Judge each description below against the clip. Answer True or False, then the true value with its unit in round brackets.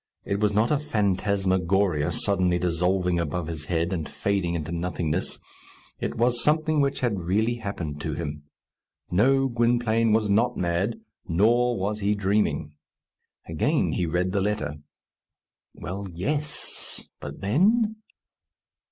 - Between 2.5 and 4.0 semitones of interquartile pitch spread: False (5.2 semitones)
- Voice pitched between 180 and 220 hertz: False (100 Hz)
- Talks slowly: True (130 wpm)